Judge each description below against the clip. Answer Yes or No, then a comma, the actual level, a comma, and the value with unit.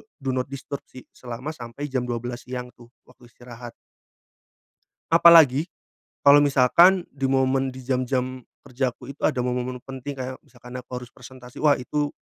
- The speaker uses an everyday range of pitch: No, narrow, 1.9 semitones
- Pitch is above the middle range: No, low, 130 Hz